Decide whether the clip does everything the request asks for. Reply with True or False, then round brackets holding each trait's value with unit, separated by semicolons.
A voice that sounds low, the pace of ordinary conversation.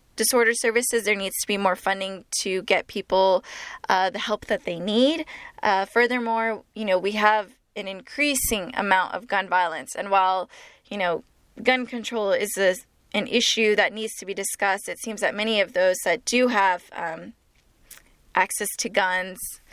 False (205 Hz; 175 wpm)